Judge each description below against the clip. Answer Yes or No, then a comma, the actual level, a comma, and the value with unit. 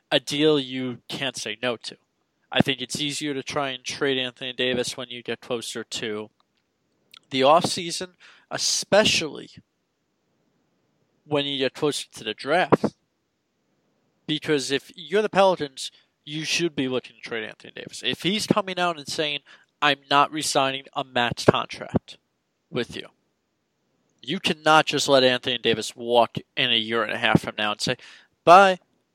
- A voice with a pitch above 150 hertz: No, medium, 140 Hz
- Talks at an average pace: Yes, average, 160 wpm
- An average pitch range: Yes, average, 3.9 semitones